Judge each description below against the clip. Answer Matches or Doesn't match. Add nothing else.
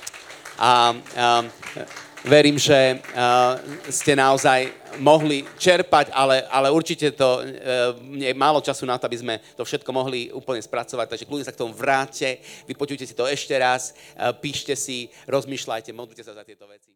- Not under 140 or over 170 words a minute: Matches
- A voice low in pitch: Matches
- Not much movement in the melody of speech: Matches